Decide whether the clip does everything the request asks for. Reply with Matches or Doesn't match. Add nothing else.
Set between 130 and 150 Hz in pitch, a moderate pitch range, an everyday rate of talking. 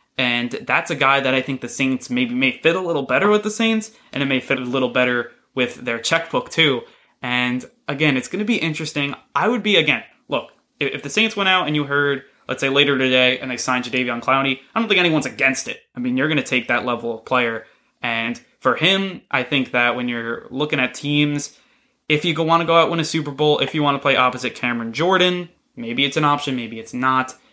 Doesn't match